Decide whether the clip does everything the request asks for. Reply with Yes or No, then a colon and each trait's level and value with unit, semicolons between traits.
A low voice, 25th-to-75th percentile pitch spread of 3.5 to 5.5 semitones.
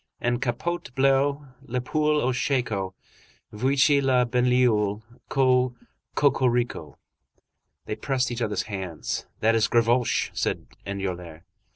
Yes: low, 125 Hz; average, 3.9 semitones